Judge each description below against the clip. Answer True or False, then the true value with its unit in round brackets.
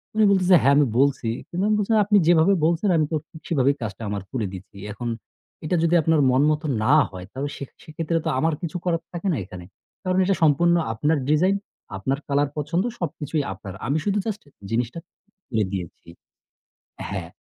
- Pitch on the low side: False (155 Hz)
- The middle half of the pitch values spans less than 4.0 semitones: False (4.8 semitones)